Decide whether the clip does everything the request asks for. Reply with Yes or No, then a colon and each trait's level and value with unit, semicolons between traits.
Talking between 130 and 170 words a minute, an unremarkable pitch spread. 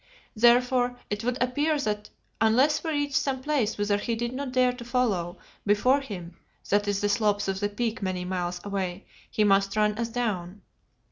No: average, 185 wpm; average, 3.8 semitones